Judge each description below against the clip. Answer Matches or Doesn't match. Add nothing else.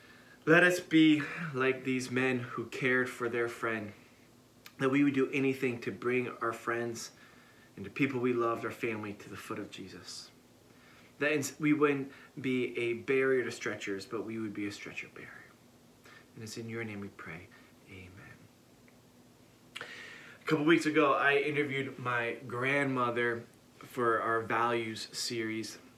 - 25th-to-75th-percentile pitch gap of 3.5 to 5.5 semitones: Doesn't match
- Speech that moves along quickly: Doesn't match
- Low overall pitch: Matches